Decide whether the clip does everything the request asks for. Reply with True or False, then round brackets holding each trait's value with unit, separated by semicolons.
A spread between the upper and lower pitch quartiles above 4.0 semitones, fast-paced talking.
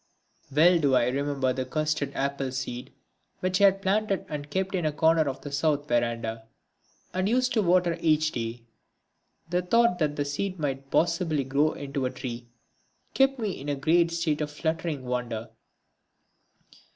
False (4.7 semitones; 165 wpm)